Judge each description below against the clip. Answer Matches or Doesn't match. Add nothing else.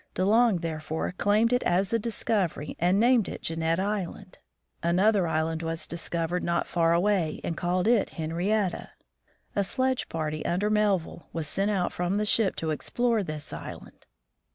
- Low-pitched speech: Doesn't match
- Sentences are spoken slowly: Doesn't match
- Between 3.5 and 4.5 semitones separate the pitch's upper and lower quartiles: Matches